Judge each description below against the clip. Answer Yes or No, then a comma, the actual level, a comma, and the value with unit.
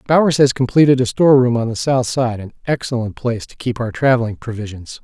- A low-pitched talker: Yes, low, 125 Hz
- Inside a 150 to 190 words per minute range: No, fast, 205 wpm